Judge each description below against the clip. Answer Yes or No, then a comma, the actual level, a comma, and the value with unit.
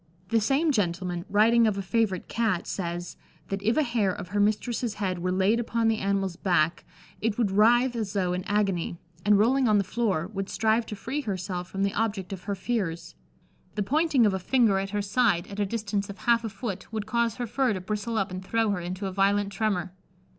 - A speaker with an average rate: No, fast, 220 wpm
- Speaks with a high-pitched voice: Yes, high, 205 Hz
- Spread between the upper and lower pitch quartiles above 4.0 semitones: No, average, 3.2 semitones